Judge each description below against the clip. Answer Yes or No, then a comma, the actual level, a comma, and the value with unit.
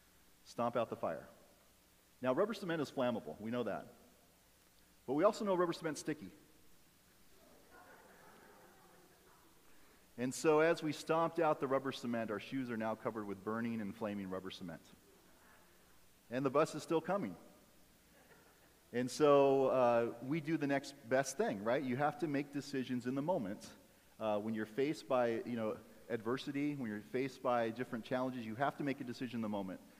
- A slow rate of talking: No, average, 170 wpm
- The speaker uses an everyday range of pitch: Yes, average, 4.3 semitones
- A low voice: Yes, low, 130 Hz